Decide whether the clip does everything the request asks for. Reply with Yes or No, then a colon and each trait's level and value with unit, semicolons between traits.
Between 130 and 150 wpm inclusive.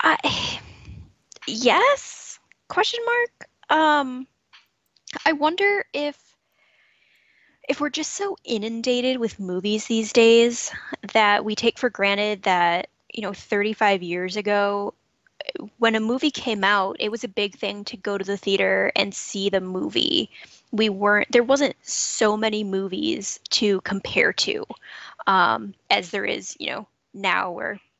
Yes: average, 140 wpm